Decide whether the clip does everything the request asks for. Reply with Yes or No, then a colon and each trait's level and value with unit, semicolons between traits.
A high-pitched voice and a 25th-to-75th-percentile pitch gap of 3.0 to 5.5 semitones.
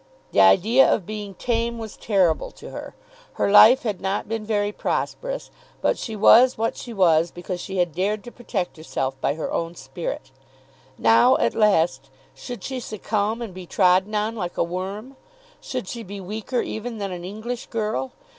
Yes: high, 205 Hz; average, 4.2 semitones